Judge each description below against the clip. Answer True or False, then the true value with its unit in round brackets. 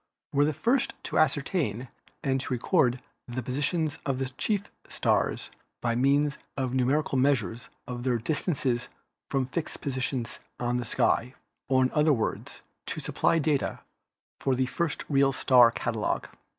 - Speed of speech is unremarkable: True (150 wpm)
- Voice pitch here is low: True (130 Hz)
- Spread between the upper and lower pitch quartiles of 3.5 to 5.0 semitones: False (2.9 semitones)